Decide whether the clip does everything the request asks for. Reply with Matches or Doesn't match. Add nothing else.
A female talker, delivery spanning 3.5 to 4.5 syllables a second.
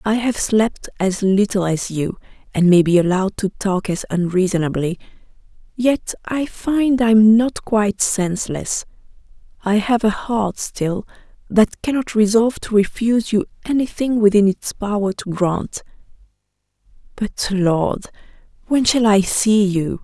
Matches